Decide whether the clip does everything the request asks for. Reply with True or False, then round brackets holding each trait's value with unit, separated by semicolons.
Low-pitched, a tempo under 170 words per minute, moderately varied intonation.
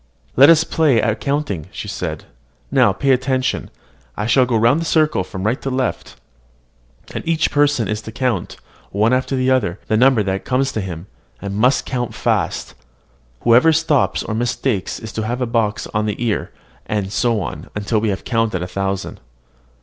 False (115 Hz; 185 wpm; 3.9 semitones)